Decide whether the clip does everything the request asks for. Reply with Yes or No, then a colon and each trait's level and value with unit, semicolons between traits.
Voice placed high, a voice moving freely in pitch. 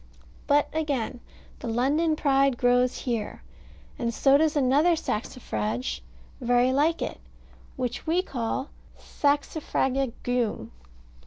No: very high, 265 Hz; average, 3.2 semitones